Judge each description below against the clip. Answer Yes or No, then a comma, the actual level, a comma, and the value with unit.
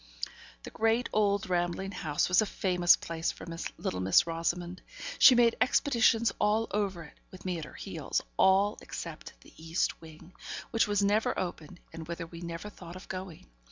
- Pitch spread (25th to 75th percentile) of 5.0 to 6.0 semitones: No, average, 3.7 semitones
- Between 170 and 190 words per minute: Yes, average, 175 wpm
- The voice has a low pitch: No, medium, 185 Hz